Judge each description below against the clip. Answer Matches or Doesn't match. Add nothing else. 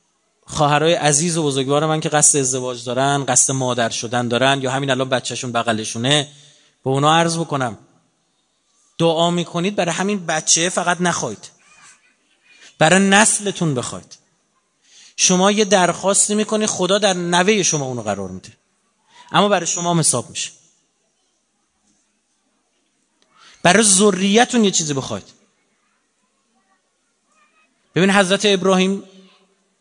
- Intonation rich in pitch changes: Matches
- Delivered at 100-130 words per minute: Matches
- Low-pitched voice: Doesn't match